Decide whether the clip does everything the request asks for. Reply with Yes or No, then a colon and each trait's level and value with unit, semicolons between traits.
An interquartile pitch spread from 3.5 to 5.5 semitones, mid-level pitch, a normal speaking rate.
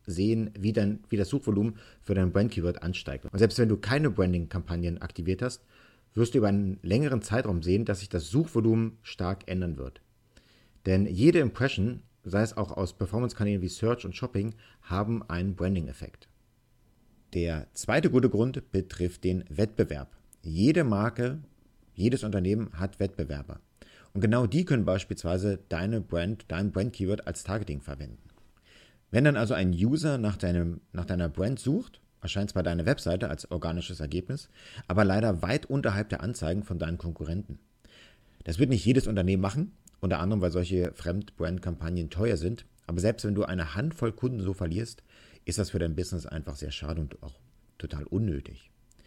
No: average, 4.2 semitones; low, 100 Hz; average, 165 wpm